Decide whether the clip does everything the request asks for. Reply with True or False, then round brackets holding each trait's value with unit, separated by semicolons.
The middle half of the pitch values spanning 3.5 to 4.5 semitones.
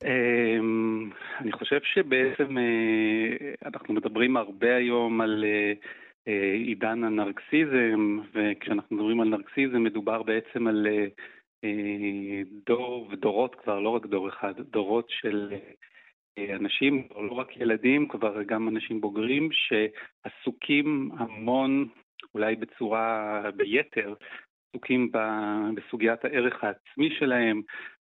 False (2.8 semitones)